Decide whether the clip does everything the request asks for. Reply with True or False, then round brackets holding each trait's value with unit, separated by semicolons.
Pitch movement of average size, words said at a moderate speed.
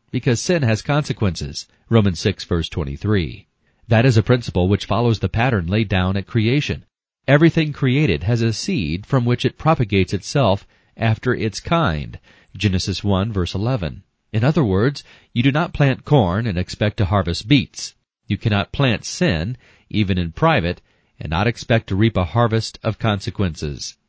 True (4.9 semitones; 165 wpm)